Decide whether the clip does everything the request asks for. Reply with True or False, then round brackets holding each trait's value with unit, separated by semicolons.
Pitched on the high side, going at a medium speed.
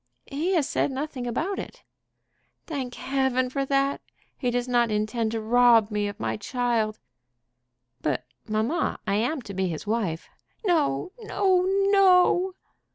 True (245 Hz; 145 wpm)